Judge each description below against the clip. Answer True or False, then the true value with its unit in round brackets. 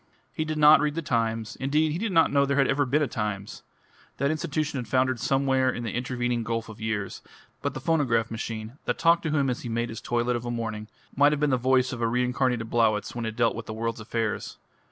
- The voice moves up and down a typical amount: True (3.7 semitones)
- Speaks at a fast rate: True (240 wpm)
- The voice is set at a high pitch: False (125 Hz)